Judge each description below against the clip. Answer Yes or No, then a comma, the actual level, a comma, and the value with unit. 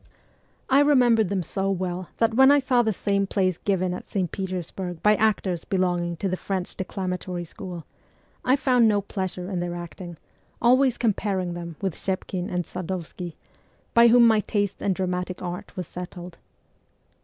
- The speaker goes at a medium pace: Yes, average, 165 wpm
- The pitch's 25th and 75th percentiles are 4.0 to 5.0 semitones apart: No, average, 3.3 semitones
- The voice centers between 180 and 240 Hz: Yes, high, 190 Hz